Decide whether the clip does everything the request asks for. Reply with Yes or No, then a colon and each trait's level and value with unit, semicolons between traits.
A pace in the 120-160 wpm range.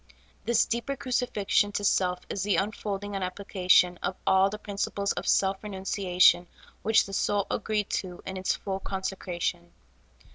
Yes: average, 155 wpm